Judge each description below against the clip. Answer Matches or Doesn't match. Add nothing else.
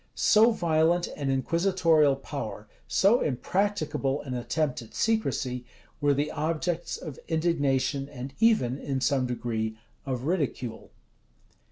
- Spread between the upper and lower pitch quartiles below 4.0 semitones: Doesn't match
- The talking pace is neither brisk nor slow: Doesn't match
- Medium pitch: Matches